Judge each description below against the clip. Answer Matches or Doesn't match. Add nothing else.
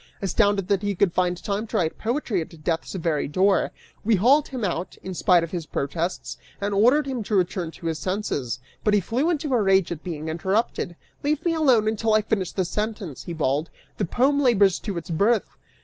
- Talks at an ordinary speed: Doesn't match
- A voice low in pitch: Doesn't match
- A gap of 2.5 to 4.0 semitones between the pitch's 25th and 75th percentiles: Doesn't match